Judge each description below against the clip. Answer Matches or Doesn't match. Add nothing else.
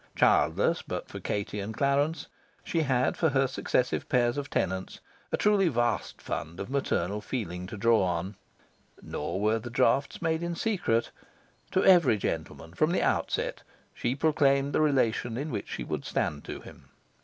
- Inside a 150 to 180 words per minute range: Matches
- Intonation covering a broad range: Matches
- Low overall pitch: Matches